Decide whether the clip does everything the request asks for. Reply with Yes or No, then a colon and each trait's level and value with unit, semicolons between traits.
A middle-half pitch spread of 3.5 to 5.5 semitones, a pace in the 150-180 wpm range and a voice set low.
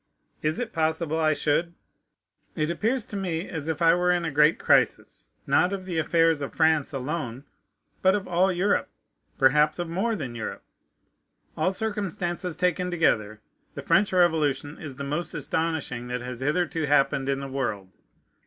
No: average, 4.2 semitones; average, 165 wpm; medium, 160 Hz